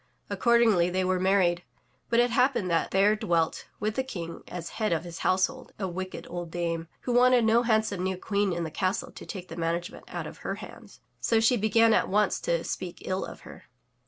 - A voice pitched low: No, high, 190 Hz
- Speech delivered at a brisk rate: Yes, fast, 210 wpm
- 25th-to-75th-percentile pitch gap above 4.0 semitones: Yes, average, 4.4 semitones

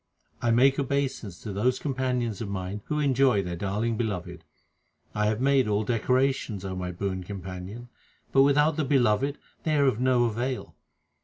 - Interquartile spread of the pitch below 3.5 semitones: No, average, 5.0 semitones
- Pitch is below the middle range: Yes, low, 120 Hz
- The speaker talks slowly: No, average, 165 wpm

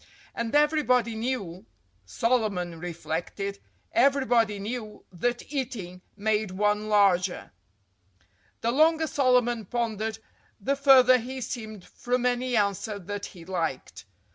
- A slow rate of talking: Yes, slow, 100 wpm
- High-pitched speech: Yes, high, 220 Hz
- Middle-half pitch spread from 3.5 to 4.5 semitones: Yes, average, 4.1 semitones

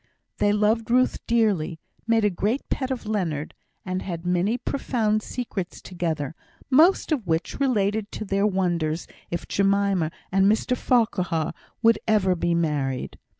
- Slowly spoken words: No, average, 145 wpm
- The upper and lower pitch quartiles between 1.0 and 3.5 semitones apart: No, average, 4.5 semitones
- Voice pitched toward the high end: Yes, high, 200 Hz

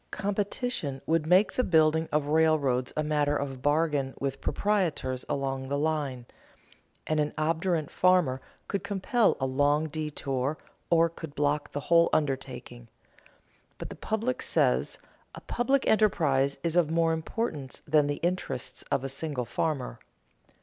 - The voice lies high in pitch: No, medium, 150 Hz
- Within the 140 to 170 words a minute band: Yes, average, 145 wpm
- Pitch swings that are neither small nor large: Yes, average, 3.5 semitones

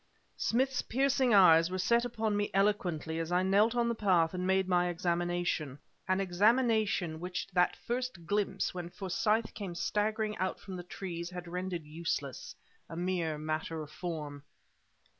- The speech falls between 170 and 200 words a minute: No, average, 160 wpm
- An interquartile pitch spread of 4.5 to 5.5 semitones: No, average, 3.7 semitones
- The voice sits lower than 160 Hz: No, medium, 185 Hz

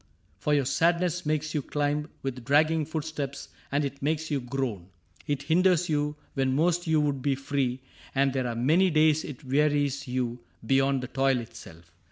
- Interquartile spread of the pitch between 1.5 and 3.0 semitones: Yes, average, 2.7 semitones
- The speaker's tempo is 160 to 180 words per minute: Yes, average, 175 wpm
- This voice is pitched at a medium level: Yes, medium, 145 Hz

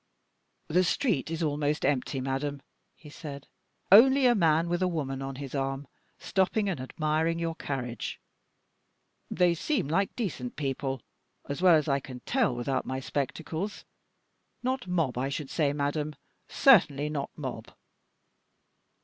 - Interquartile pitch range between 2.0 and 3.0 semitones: No, average, 4.3 semitones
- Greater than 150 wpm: No, average, 140 wpm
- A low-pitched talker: No, medium, 150 Hz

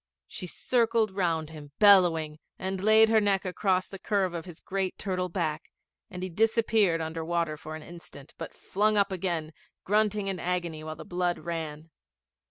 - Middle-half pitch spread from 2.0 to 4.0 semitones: Yes, average, 3.7 semitones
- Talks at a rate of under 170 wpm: No, average, 175 wpm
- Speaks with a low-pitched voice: No, medium, 180 Hz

